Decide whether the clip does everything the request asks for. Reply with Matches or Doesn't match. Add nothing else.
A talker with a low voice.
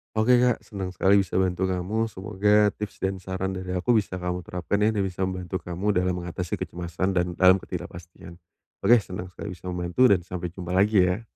Matches